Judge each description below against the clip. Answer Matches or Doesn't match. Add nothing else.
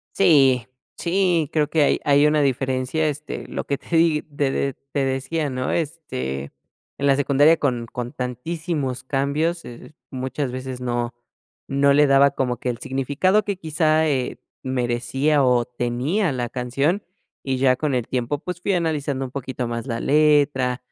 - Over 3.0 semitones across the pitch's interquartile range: Matches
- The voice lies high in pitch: Doesn't match